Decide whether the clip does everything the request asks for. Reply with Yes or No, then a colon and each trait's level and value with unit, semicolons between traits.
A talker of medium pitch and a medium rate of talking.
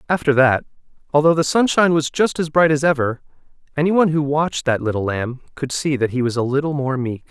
No: medium, 145 Hz; fast, 220 wpm